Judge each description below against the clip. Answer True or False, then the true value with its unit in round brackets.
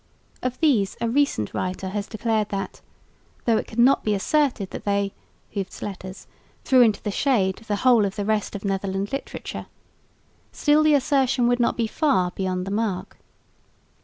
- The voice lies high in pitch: True (215 Hz)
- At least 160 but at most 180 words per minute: True (170 wpm)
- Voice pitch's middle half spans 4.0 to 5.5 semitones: True (4.3 semitones)